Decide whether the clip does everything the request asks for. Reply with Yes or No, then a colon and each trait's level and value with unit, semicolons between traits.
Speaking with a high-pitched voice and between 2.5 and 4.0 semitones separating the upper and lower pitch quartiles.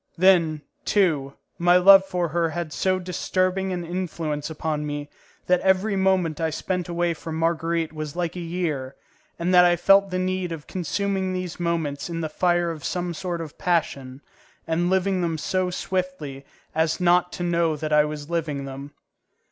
No: medium, 170 Hz; average, 2.8 semitones